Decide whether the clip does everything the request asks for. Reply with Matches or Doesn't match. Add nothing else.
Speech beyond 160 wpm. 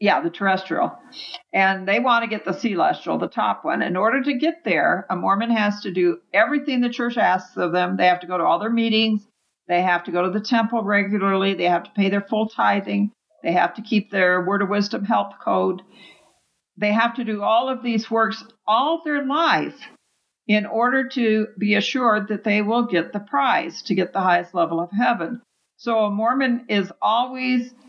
Matches